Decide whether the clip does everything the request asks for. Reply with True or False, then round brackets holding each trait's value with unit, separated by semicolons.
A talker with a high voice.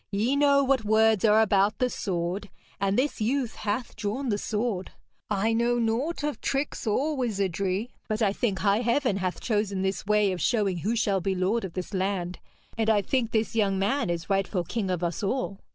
True (210 Hz)